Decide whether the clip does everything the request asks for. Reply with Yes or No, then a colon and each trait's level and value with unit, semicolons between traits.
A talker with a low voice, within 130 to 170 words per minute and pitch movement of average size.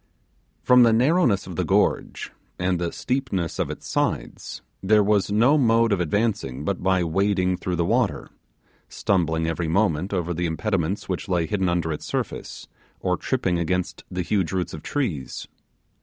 Yes: very low, 95 Hz; average, 165 wpm; average, 3.7 semitones